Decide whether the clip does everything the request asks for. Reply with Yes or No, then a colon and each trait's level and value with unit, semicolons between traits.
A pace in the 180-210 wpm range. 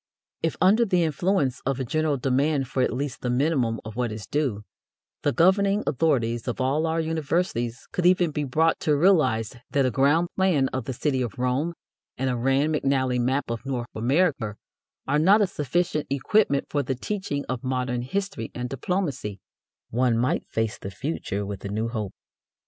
Yes: average, 185 wpm